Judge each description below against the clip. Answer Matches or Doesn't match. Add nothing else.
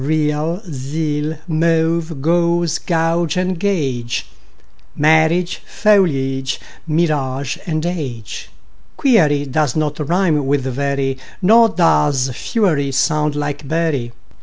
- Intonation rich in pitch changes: Doesn't match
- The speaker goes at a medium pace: Doesn't match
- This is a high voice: Doesn't match